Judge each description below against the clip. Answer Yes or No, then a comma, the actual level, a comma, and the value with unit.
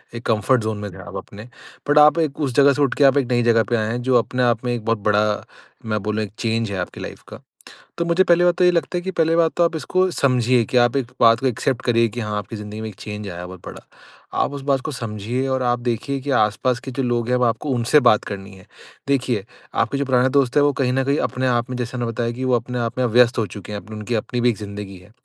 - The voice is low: Yes, low, 120 Hz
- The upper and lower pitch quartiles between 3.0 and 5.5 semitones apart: Yes, average, 3.6 semitones